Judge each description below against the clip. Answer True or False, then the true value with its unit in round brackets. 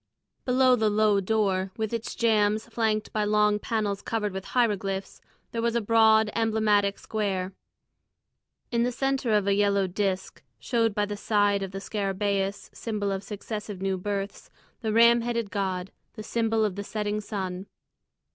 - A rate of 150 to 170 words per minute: True (160 wpm)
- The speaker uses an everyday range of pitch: False (2.1 semitones)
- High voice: True (210 Hz)